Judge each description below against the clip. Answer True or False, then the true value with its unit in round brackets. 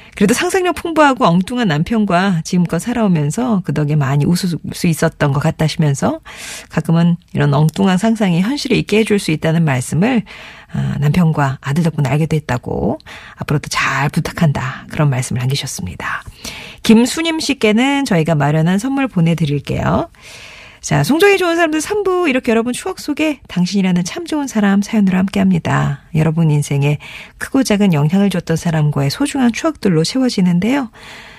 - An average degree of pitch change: False (7.0 semitones)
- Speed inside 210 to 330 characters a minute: False (365 characters per minute)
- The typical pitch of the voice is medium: True (180 Hz)